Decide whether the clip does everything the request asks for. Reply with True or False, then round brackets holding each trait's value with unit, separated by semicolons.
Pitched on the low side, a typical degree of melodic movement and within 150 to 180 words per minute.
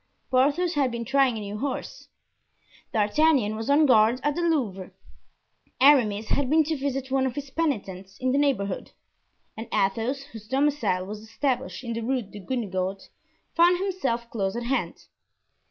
False (255 Hz; 4.9 semitones; 155 wpm)